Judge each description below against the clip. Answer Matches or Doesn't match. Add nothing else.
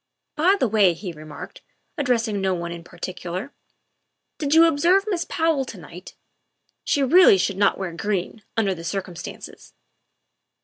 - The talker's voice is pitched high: Matches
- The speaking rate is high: Doesn't match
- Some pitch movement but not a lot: Doesn't match